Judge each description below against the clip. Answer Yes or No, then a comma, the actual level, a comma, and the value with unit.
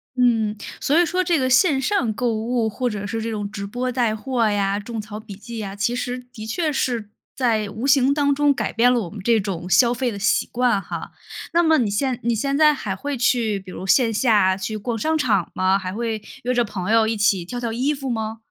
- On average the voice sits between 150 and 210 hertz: No, high, 230 Hz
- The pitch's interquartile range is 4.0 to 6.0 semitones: No, average, 3.5 semitones